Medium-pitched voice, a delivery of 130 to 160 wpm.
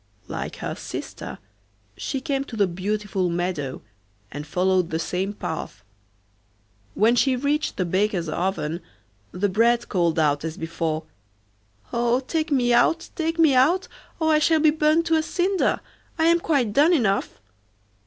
No: high, 225 Hz; average, 155 wpm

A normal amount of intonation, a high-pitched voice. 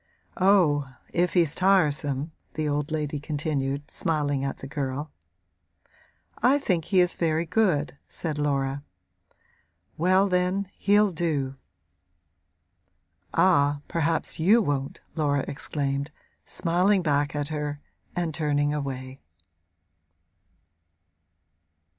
No: average, 3.6 semitones; medium, 150 Hz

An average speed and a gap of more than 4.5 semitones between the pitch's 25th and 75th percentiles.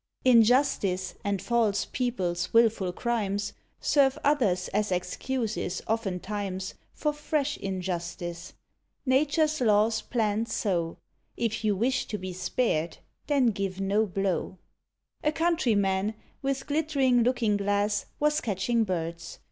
No: slow, 115 wpm; average, 5.0 semitones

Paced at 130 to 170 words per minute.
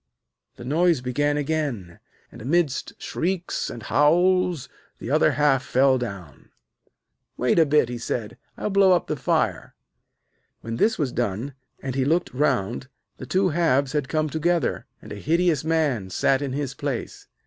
Yes: average, 160 wpm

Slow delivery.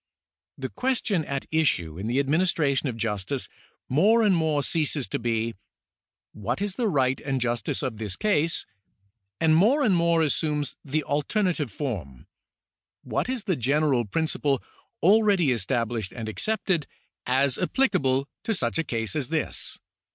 No: average, 155 wpm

